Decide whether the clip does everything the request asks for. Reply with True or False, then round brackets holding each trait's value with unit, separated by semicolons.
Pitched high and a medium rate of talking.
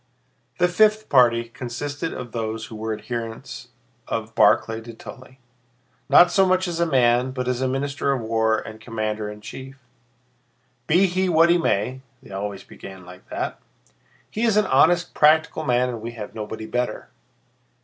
False (125 Hz; 165 wpm)